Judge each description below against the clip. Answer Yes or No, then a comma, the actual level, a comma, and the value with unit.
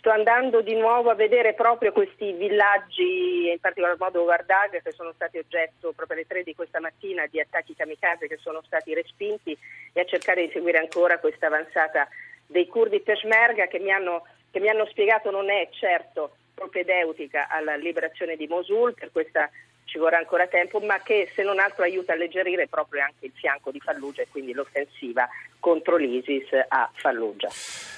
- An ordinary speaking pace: No, fast, 175 wpm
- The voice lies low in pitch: No, medium, 185 Hz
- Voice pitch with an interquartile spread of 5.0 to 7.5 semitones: Yes, average, 5.3 semitones